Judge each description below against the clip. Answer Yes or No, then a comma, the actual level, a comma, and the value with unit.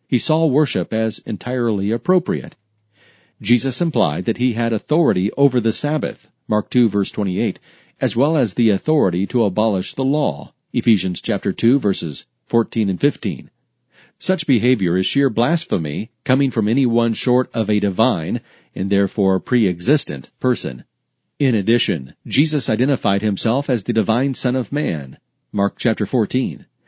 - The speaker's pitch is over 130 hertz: No, low, 115 Hz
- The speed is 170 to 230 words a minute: No, average, 145 wpm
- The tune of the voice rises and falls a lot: No, average, 4.2 semitones